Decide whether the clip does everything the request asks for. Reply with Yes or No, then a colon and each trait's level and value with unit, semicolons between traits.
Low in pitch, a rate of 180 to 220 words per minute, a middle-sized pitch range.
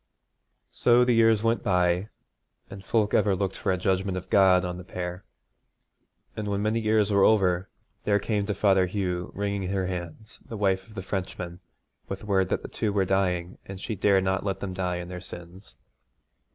No: very low, 95 Hz; average, 190 wpm; narrow, 2.1 semitones